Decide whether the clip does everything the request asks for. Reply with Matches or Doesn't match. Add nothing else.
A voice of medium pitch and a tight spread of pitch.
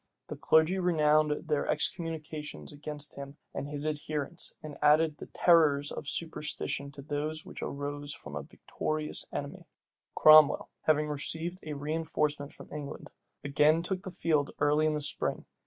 Matches